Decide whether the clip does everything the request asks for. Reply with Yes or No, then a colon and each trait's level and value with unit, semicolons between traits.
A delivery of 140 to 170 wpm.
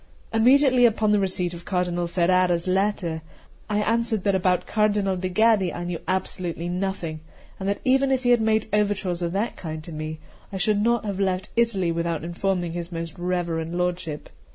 No: average, 180 wpm